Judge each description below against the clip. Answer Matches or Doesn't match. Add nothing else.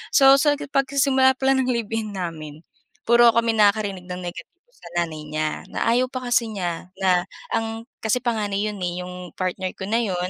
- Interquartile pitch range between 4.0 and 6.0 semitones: Matches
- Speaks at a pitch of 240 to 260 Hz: Doesn't match